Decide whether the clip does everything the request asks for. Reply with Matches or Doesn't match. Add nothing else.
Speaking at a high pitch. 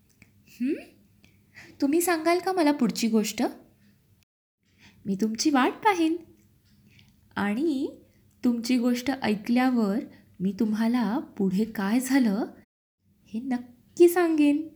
Matches